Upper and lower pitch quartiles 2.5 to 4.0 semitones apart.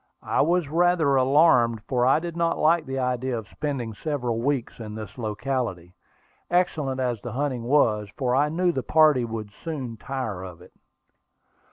No: average, 4.5 semitones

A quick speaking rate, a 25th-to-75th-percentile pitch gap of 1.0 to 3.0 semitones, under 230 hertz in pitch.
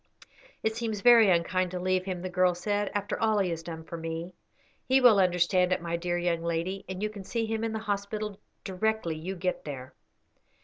No: fast, 210 wpm; average, 3.5 semitones; medium, 185 Hz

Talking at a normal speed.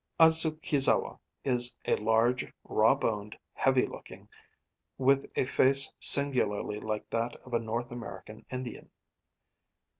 No: slow, 110 wpm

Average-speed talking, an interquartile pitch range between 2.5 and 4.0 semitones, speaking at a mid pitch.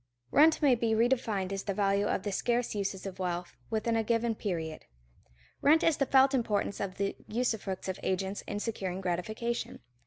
No: average, 180 wpm; average, 3.7 semitones; high, 210 Hz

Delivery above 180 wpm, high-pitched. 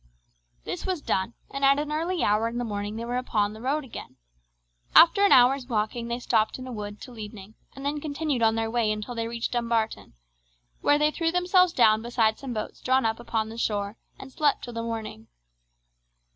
Yes: fast, 205 wpm; high, 235 Hz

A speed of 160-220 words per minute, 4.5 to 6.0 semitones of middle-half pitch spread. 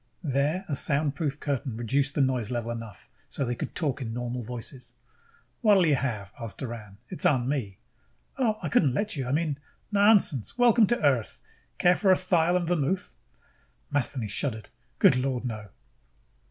Yes: average, 170 wpm; wide, 5.6 semitones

